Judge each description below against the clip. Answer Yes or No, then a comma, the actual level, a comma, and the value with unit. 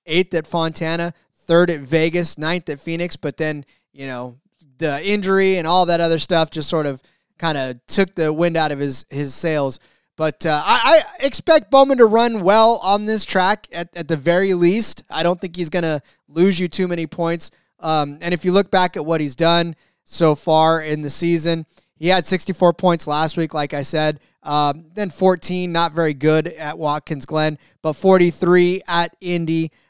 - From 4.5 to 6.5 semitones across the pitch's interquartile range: No, average, 2.8 semitones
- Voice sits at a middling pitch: Yes, medium, 170 Hz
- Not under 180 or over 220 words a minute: Yes, average, 200 wpm